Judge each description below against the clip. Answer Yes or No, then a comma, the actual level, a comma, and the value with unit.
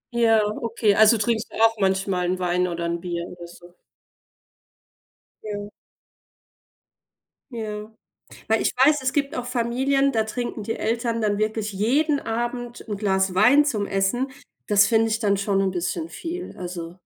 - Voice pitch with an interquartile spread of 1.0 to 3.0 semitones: No, average, 3.7 semitones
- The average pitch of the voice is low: No, high, 215 Hz